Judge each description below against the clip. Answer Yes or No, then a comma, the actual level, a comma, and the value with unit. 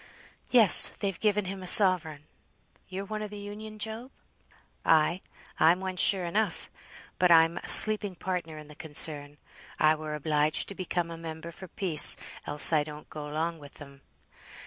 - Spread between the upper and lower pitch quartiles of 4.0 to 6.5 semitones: Yes, average, 4.3 semitones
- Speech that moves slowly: No, average, 170 wpm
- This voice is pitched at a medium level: Yes, medium, 170 Hz